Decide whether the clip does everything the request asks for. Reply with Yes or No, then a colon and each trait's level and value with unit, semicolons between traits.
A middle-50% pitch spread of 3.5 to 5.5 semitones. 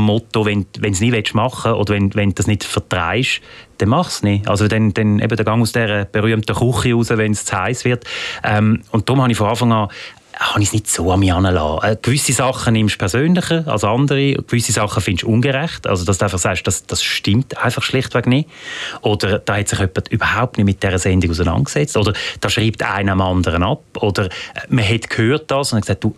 No: average, 3.0 semitones